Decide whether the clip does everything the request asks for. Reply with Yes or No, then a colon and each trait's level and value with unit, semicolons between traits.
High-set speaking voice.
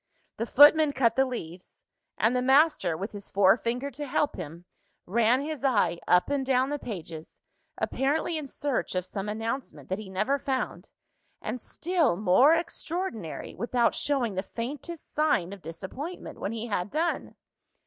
Yes: high, 240 Hz